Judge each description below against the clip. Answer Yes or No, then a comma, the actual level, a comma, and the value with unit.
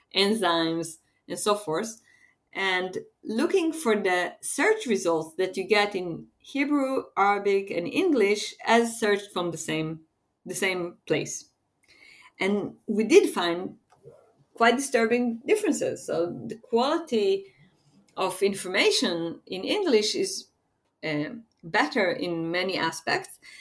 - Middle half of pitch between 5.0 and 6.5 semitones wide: Yes, average, 5.3 semitones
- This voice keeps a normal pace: No, slow, 115 wpm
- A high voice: Yes, high, 200 Hz